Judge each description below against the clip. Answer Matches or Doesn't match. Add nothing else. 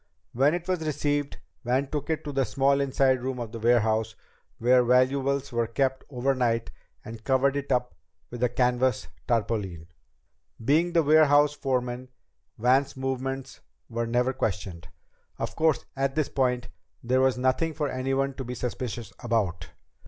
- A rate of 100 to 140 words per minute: Doesn't match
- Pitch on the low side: Matches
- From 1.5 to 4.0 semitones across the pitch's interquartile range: Matches